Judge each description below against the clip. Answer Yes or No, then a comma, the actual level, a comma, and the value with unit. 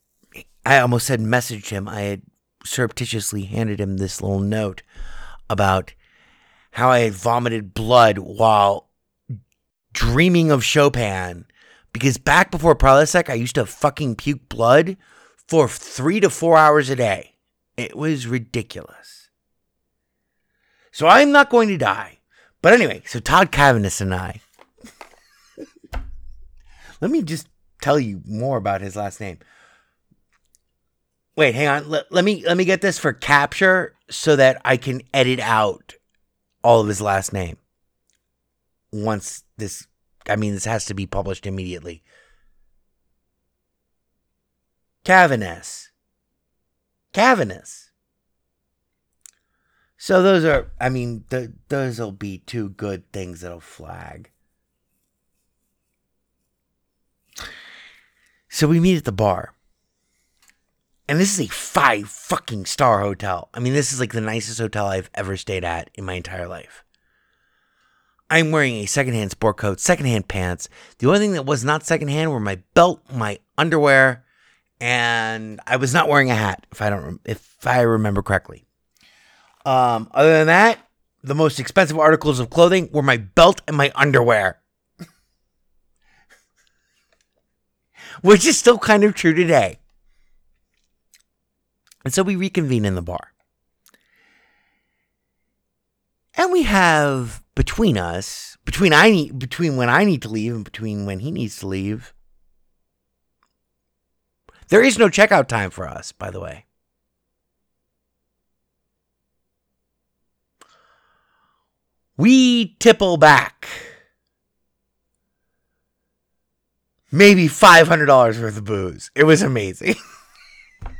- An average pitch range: No, wide, 8.4 semitones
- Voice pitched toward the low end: Yes, low, 115 Hz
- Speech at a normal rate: No, slow, 125 wpm